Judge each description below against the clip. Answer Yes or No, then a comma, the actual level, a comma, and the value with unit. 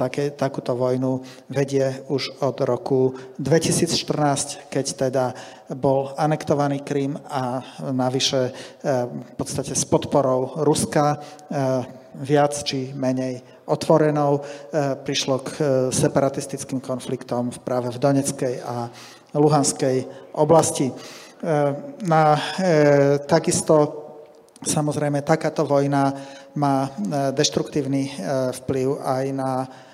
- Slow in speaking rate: Yes, slow, 85 wpm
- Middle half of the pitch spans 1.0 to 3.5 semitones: Yes, narrow, 2.4 semitones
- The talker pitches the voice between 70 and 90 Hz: No, medium, 140 Hz